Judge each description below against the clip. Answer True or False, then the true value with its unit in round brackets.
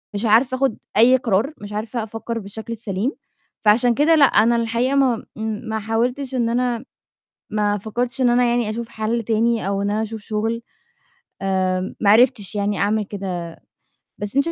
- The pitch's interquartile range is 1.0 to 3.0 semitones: True (2.7 semitones)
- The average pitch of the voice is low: False (225 Hz)